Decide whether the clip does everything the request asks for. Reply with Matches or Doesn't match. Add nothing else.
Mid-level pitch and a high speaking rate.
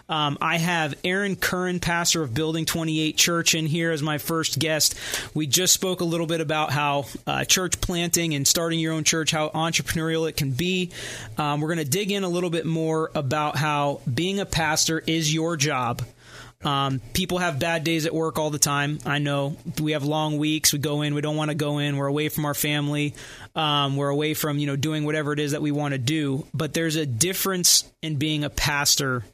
Matches